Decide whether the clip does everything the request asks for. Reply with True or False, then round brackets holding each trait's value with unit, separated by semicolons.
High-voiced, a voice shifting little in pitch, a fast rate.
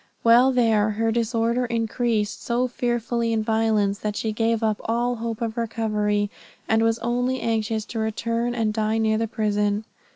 False (225 Hz; 1.5 semitones; 165 wpm)